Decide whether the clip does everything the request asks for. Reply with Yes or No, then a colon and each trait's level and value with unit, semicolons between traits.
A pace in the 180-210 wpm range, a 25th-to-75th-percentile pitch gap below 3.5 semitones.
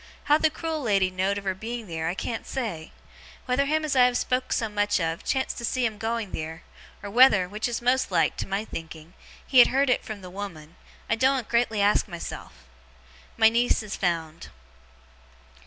No: average, 200 wpm; average, 5.2 semitones